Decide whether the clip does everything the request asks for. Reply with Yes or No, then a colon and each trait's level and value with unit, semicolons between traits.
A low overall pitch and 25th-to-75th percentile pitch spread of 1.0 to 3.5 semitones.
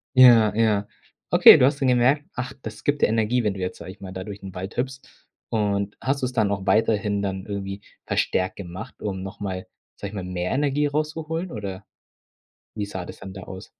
No: low, 105 Hz; average, 4.8 semitones